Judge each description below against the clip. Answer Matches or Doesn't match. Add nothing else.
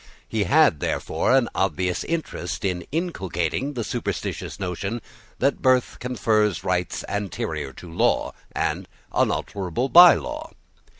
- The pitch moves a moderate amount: Doesn't match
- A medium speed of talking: Doesn't match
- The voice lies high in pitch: Doesn't match